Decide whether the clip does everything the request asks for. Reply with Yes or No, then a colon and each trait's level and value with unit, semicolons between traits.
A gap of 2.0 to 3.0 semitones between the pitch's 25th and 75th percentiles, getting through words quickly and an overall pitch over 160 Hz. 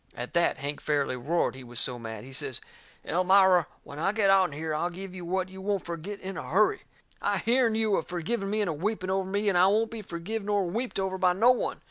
No: average, 4.2 semitones; fast, 245 wpm; medium, 185 Hz